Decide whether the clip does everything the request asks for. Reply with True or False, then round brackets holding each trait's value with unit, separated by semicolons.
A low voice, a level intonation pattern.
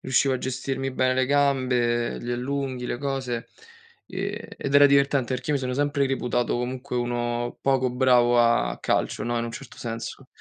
True (130 Hz; 2.1 semitones)